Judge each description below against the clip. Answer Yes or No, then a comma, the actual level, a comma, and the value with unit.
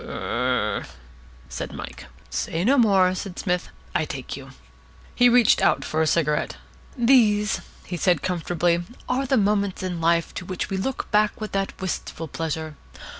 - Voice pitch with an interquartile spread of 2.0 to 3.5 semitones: No, average, 4.2 semitones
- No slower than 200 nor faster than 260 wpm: No, average, 165 wpm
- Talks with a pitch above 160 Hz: Yes, medium, 185 Hz